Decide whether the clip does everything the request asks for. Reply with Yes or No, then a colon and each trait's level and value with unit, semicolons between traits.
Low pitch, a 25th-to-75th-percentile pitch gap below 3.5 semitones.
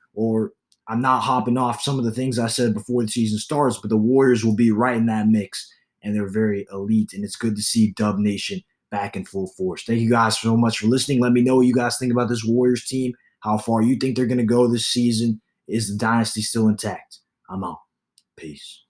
Yes: low, 115 Hz; narrow, 2.4 semitones